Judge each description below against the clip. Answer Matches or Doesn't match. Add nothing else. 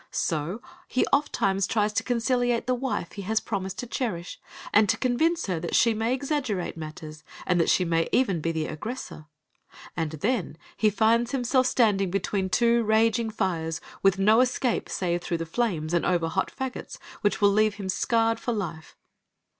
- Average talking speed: Matches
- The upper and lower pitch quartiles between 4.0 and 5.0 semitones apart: Doesn't match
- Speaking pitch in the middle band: Doesn't match